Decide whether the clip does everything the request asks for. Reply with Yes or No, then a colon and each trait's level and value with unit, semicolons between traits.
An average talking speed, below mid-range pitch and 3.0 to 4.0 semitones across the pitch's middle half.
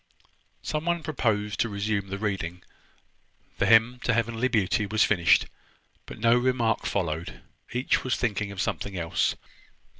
Yes: average, 145 wpm; low, 110 Hz; average, 3.5 semitones